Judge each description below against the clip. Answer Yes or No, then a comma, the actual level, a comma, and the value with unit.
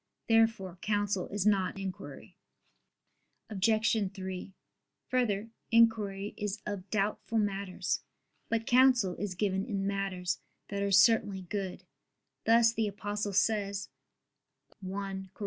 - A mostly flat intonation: Yes, narrow, 2.2 semitones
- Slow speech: Yes, slow, 115 wpm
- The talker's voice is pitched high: Yes, high, 200 Hz